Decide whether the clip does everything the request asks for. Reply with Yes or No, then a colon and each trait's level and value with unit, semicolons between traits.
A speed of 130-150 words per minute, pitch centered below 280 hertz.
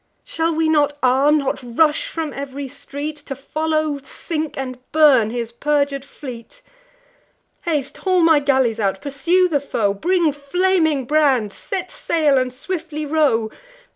No: average, 140 wpm; very high, 290 Hz